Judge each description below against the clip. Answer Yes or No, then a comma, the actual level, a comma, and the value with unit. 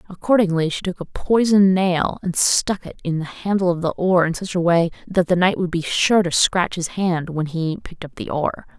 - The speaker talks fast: Yes, fast, 240 wpm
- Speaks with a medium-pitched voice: Yes, medium, 180 Hz